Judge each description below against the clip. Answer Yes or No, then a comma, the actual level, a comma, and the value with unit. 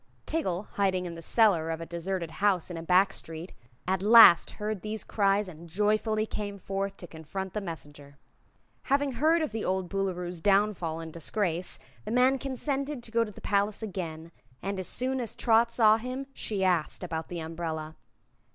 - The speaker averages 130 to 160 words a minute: No, average, 180 wpm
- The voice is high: Yes, high, 195 Hz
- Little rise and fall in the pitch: No, average, 4.3 semitones